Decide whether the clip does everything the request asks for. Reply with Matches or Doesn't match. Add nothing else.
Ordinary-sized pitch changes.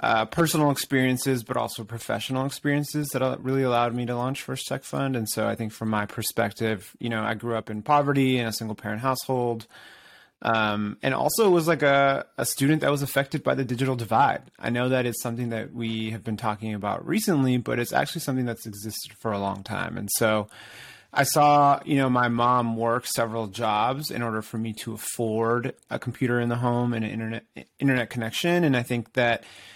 Matches